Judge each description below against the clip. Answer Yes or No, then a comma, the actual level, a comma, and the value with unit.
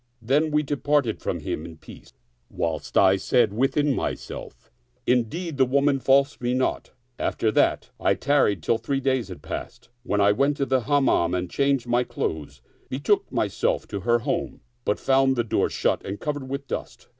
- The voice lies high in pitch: No, low, 130 Hz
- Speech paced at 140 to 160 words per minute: No, average, 180 wpm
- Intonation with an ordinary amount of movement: Yes, average, 4.5 semitones